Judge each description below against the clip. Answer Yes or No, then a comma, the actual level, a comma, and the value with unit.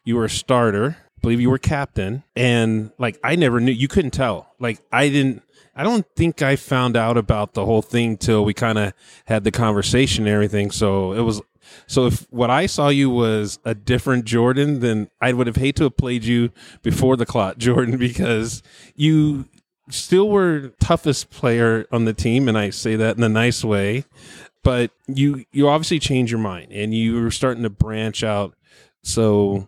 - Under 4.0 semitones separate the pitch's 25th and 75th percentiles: Yes, average, 3.5 semitones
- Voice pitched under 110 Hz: No, low, 120 Hz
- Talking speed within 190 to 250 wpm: Yes, average, 200 wpm